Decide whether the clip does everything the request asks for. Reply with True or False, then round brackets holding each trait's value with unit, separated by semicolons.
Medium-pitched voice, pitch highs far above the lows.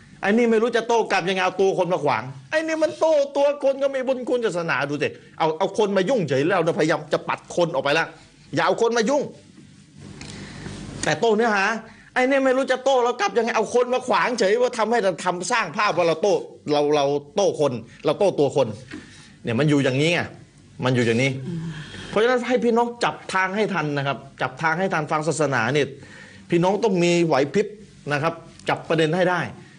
True (180 Hz; 7.5 semitones)